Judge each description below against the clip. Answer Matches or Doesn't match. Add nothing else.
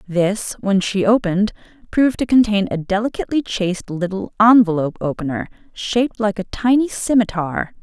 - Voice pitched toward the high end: Matches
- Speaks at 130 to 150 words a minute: Matches